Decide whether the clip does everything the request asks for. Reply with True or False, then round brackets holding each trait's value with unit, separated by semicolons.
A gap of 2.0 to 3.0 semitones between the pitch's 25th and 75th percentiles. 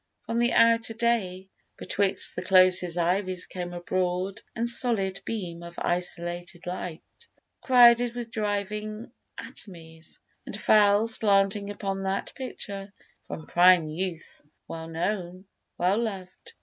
False (3.4 semitones)